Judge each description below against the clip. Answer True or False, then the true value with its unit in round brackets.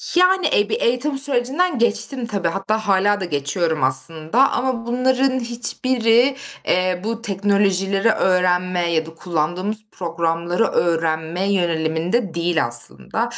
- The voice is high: True (195 Hz)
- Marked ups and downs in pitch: True (5.9 semitones)